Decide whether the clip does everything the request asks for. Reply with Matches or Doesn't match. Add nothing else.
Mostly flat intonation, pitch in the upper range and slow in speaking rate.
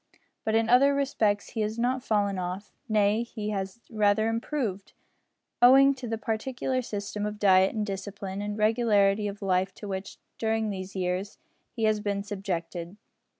Doesn't match